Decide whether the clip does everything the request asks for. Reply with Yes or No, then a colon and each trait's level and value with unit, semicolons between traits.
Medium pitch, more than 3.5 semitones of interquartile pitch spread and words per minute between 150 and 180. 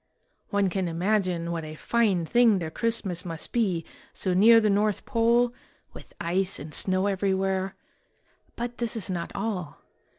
No: high, 195 Hz; average, 4.2 semitones; average, 160 wpm